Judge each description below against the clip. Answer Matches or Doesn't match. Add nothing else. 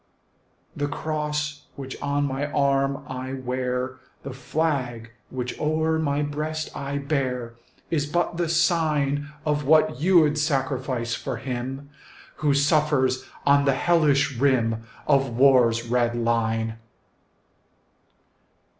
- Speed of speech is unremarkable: Doesn't match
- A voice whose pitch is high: Doesn't match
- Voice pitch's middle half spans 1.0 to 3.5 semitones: Matches